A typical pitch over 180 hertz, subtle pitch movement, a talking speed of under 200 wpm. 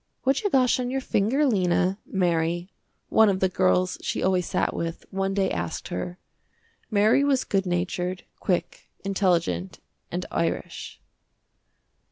No: high, 190 Hz; average, 3.6 semitones; average, 140 wpm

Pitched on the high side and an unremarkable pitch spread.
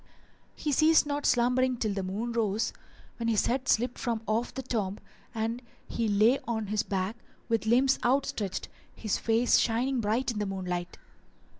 Yes: high, 230 Hz; average, 3.1 semitones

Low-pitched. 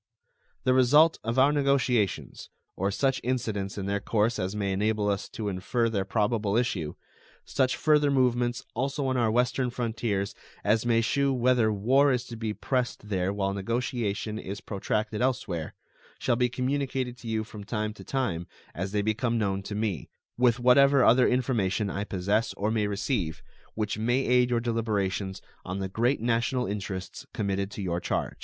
Yes: low, 110 Hz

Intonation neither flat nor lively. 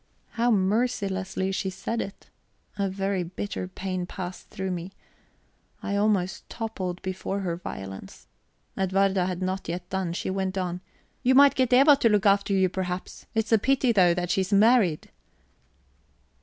No: narrow, 2.3 semitones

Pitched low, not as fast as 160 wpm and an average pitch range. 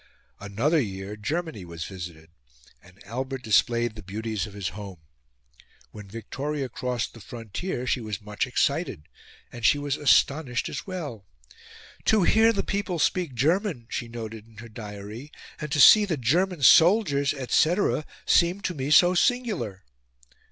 No: low, 125 Hz; average, 150 wpm; wide, 7.2 semitones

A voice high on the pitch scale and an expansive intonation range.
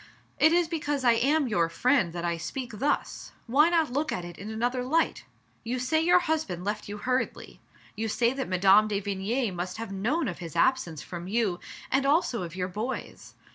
Yes: high, 230 Hz; wide, 6.4 semitones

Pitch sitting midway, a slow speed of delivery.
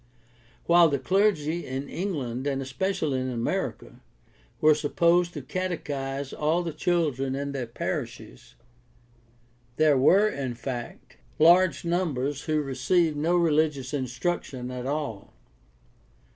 Yes: medium, 145 Hz; slow, 115 wpm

